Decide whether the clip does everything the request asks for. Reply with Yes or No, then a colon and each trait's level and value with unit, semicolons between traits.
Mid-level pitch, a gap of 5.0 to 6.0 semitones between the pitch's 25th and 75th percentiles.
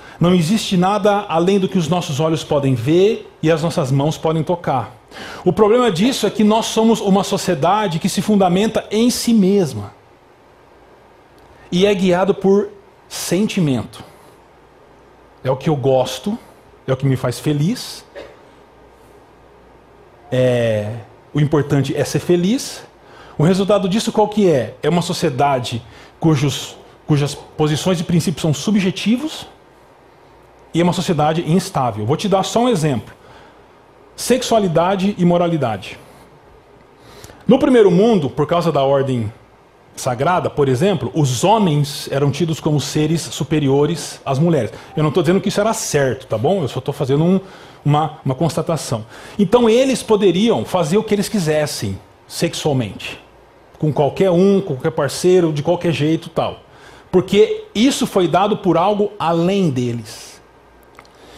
Yes: medium, 170 Hz; wide, 5.6 semitones